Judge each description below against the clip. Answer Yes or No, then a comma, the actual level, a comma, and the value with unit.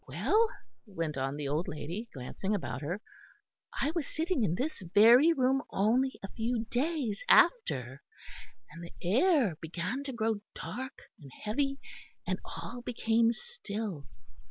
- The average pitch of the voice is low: No, high, 220 Hz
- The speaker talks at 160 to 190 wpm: No, average, 140 wpm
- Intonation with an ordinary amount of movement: No, wide, 7.7 semitones